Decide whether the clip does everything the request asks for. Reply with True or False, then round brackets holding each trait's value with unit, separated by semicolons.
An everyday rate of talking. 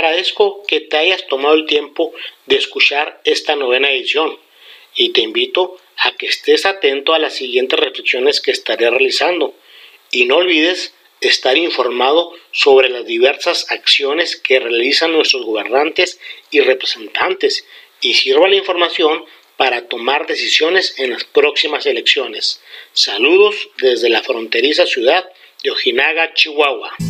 True (135 wpm)